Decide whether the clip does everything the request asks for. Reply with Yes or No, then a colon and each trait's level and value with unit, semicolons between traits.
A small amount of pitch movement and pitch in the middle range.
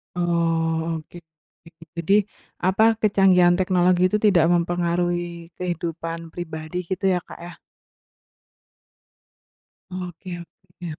Yes: narrow, 1.5 semitones; medium, 175 Hz